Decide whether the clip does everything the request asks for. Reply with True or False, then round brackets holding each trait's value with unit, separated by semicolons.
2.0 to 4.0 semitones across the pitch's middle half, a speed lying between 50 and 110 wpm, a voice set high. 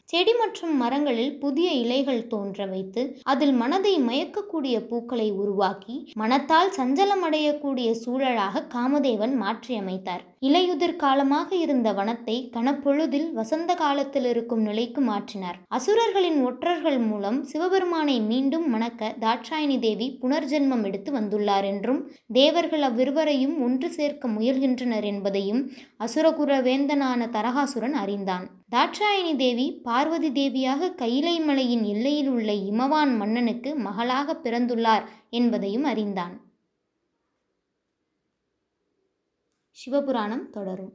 False (4.6 semitones; 95 wpm; 260 Hz)